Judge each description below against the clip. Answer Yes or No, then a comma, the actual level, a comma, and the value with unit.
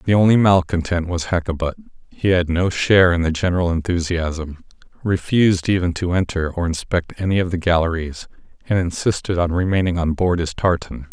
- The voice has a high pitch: No, very low, 90 Hz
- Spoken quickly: No, average, 165 wpm